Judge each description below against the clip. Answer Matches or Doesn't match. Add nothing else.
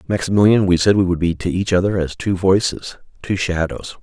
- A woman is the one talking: Doesn't match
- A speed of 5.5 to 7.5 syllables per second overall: Matches